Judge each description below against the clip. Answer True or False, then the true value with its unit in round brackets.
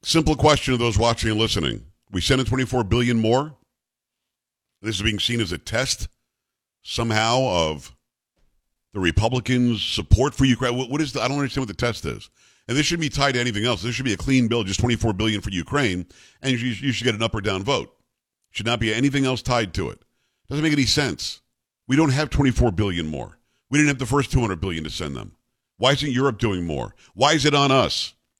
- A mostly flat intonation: False (3.8 semitones)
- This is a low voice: True (120 Hz)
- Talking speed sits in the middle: False (220 wpm)